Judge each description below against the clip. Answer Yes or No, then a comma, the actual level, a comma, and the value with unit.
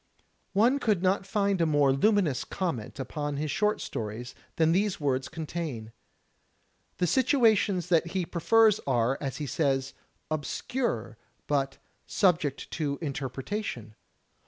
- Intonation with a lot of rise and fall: Yes, wide, 6.4 semitones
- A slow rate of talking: Yes, slow, 125 wpm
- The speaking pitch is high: No, medium, 160 Hz